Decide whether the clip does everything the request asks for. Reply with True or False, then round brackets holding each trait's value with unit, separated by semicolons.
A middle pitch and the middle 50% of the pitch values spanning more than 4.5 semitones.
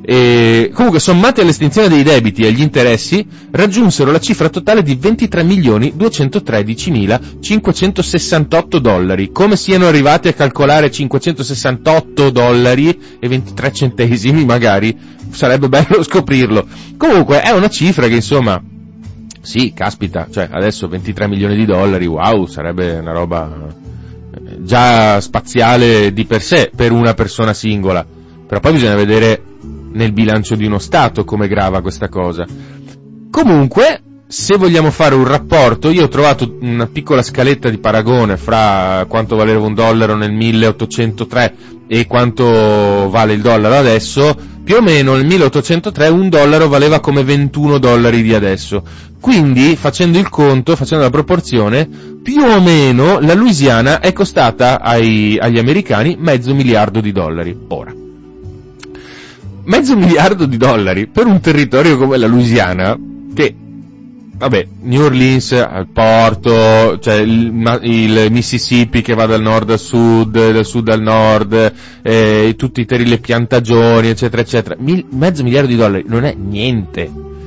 False (120 Hz; 5.2 semitones)